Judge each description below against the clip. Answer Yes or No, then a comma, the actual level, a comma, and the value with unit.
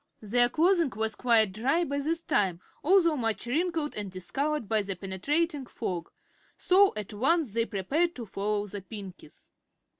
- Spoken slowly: No, average, 155 wpm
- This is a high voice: Yes, high, 235 Hz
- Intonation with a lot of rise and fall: Yes, wide, 7.4 semitones